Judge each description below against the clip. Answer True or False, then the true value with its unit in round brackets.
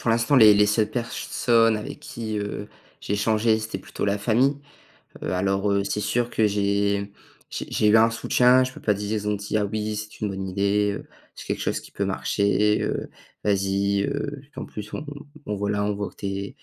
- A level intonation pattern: True (1.8 semitones)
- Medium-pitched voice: False (105 Hz)